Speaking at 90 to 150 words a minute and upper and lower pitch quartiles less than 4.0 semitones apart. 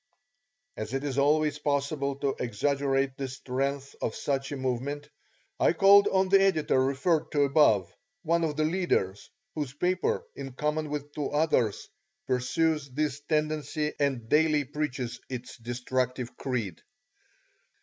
Yes: average, 140 wpm; average, 2.9 semitones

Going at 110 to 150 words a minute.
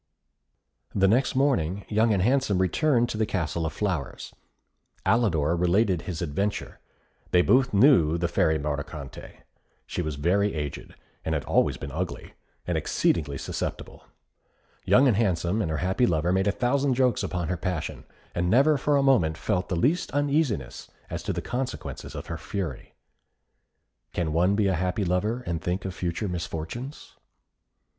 No: average, 160 wpm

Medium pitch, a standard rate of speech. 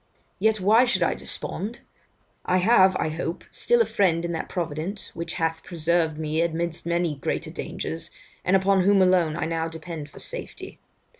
Yes: medium, 170 Hz; average, 170 wpm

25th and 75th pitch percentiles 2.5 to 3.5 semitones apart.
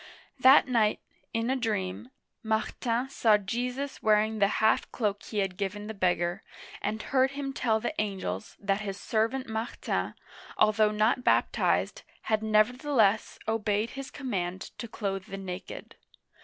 Yes: average, 3.2 semitones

